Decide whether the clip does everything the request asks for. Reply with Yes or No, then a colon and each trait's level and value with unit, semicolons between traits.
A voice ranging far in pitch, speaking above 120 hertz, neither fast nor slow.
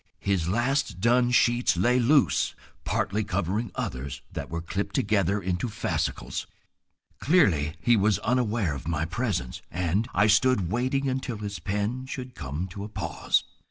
No: wide, 5.7 semitones; low, 100 Hz; average, 150 wpm